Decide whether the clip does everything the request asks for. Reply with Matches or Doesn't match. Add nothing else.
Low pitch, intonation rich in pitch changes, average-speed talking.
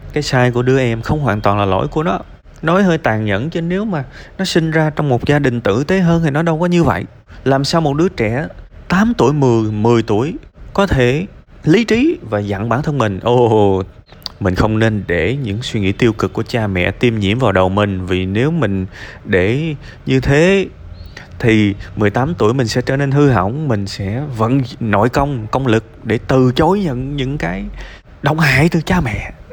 Matches